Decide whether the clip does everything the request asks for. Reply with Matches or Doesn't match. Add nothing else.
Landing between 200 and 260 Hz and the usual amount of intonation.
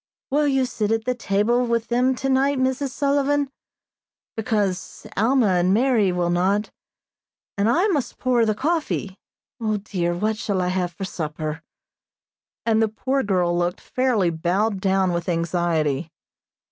Doesn't match